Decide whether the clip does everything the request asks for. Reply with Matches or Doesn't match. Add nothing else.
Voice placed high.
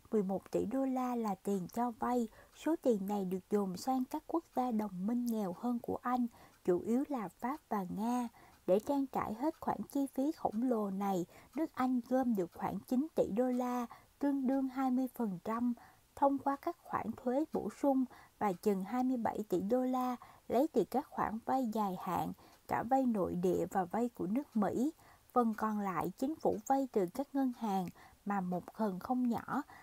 Matches